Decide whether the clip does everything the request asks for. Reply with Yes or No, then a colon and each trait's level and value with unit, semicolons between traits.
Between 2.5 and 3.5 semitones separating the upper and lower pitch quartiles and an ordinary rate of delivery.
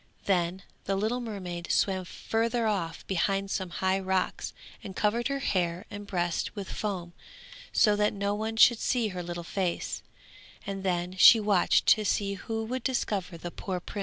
Yes: average, 3.0 semitones; average, 170 wpm